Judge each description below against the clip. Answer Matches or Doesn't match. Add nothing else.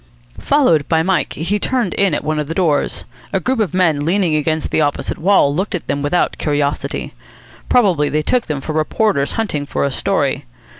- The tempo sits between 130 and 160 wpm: Doesn't match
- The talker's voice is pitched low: Doesn't match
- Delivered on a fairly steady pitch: Doesn't match